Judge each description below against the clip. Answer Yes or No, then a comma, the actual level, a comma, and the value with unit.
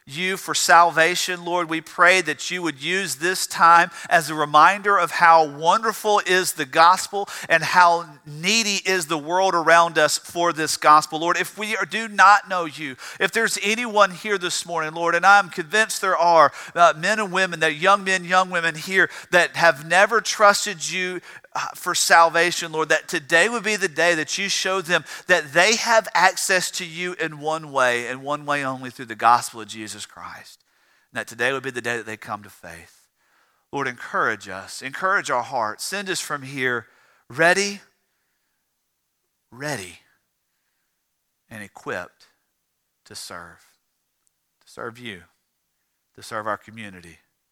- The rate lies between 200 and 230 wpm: No, average, 170 wpm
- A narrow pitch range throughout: No, average, 3.9 semitones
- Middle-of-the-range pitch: Yes, medium, 170 Hz